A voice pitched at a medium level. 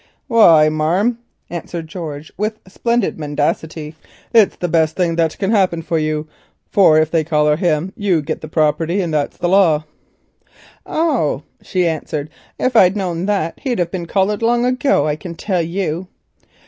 Yes: medium, 170 Hz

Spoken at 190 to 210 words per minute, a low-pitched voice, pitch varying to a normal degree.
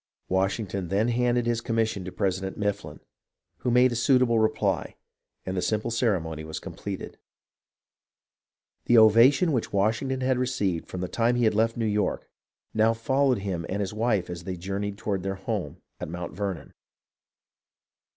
No: average, 160 wpm; low, 105 Hz; average, 3.7 semitones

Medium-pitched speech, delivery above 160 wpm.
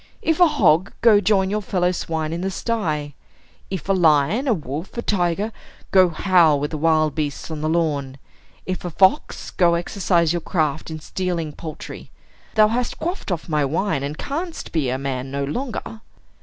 Yes: medium, 170 Hz; average, 180 wpm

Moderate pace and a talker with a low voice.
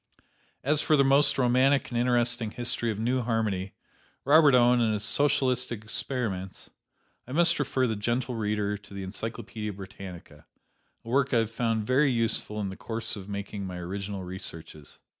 Yes: average, 165 wpm; low, 115 Hz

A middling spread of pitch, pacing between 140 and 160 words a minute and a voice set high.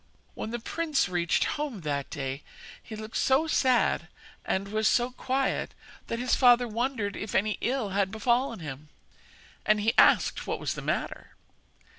Yes: average, 4.7 semitones; average, 155 wpm; high, 220 Hz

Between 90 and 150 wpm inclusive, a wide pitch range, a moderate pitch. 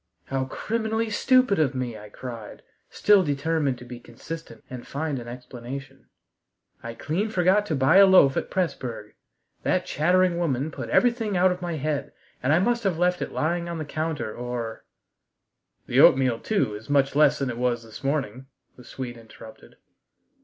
No: average, 175 wpm; wide, 6.2 semitones; medium, 145 Hz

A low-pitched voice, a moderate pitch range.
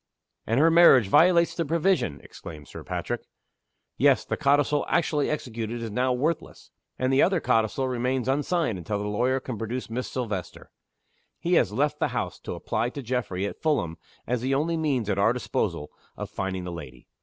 No: low, 125 Hz; wide, 5.9 semitones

